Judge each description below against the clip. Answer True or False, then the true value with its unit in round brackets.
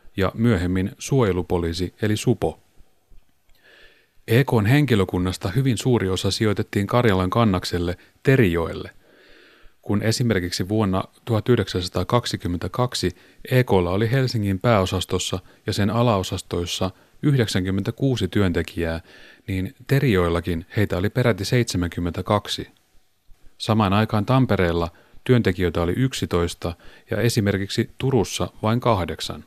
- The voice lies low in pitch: True (100 Hz)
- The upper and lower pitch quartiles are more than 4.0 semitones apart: True (4.4 semitones)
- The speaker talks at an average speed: False (90 wpm)